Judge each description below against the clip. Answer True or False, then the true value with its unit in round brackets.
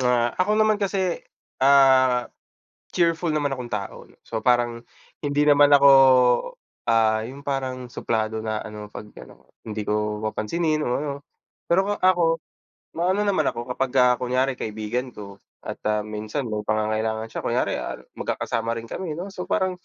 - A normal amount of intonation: False (5.8 semitones)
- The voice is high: False (125 Hz)